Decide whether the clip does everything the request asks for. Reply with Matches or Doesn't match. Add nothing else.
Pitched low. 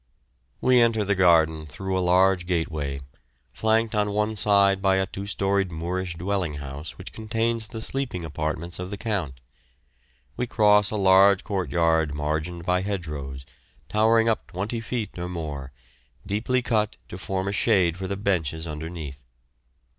Matches